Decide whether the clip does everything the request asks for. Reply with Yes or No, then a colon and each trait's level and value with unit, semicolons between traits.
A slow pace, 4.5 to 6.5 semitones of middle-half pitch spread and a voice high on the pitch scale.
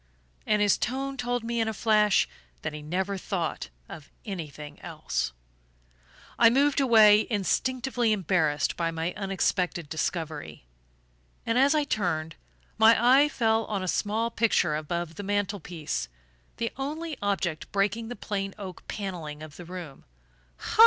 No: average, 145 wpm; wide, 5.5 semitones; high, 200 Hz